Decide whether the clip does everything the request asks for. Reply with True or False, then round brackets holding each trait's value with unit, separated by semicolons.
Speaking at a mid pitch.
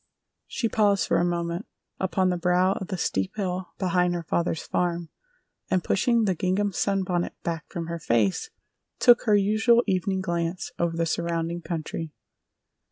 True (180 Hz)